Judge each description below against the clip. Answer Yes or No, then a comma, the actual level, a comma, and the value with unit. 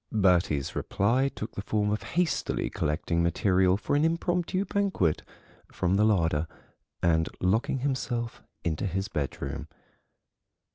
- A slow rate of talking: Yes, slow, 125 wpm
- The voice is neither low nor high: No, low, 100 Hz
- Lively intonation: Yes, wide, 7.7 semitones